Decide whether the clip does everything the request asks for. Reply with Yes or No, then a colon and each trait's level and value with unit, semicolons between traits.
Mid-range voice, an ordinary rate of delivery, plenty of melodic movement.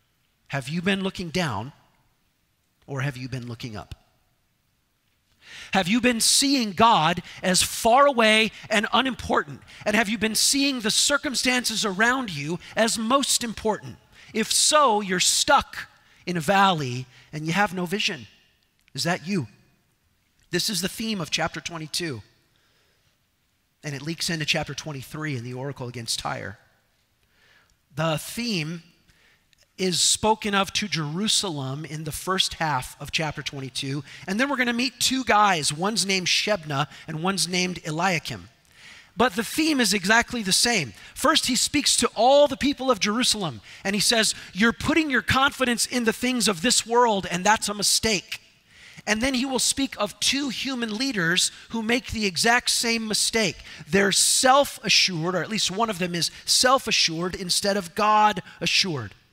No: high, 195 Hz; average, 160 wpm; wide, 6.7 semitones